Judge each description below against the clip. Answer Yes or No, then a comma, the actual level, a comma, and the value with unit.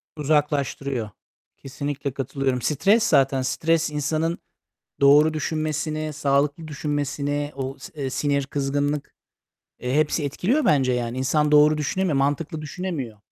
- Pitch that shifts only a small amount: Yes, narrow, 2.0 semitones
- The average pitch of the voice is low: No, medium, 145 Hz